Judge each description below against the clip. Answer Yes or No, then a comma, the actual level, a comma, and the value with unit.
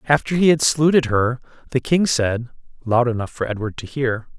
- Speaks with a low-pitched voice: Yes, low, 130 Hz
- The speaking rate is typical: Yes, average, 190 wpm